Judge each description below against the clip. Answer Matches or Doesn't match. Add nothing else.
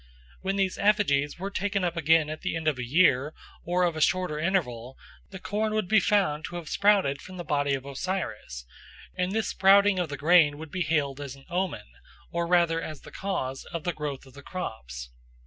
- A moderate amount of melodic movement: Matches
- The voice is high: Doesn't match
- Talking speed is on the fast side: Matches